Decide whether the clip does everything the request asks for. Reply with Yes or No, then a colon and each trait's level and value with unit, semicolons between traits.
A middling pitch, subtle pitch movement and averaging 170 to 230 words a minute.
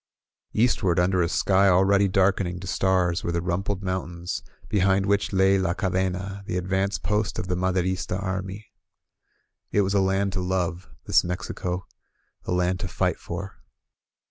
No: very low, 95 Hz; narrow, 1.4 semitones; average, 180 wpm